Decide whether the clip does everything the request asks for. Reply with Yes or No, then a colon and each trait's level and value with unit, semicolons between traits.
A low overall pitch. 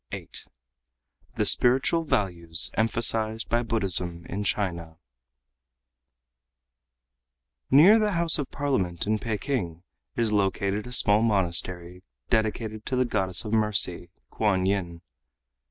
Yes: low, 105 Hz